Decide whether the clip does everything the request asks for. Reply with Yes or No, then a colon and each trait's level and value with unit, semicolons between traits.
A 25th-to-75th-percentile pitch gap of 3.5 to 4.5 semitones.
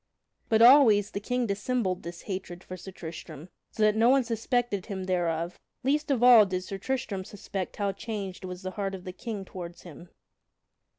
Yes: average, 3.9 semitones